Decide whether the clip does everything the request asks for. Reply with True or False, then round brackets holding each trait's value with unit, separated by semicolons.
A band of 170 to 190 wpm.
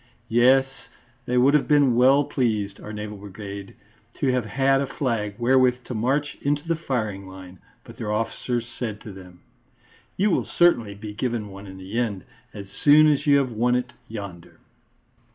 True (175 wpm)